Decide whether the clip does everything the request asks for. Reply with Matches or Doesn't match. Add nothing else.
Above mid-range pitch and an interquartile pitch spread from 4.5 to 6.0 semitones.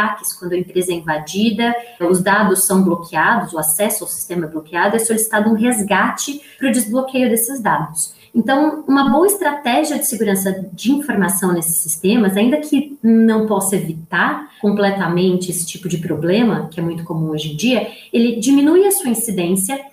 Matches